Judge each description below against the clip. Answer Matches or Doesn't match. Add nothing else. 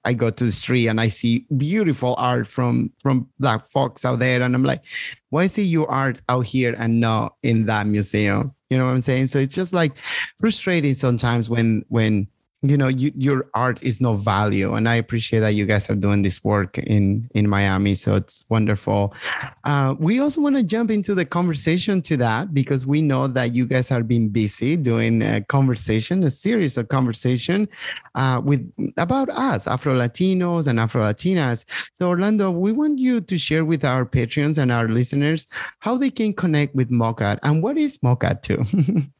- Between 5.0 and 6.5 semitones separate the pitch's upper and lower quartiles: Matches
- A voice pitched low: Matches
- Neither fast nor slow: Matches